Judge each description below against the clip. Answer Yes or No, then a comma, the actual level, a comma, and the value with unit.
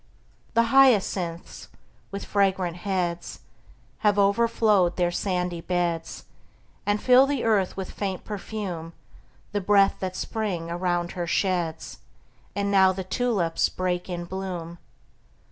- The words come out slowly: Yes, slow, 120 wpm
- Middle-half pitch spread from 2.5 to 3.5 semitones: Yes, average, 2.8 semitones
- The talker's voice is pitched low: No, high, 190 Hz